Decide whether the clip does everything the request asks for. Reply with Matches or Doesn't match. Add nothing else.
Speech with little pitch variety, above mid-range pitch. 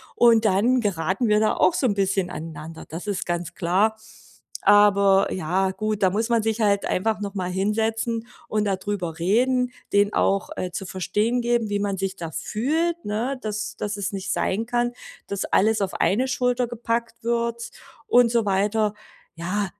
Doesn't match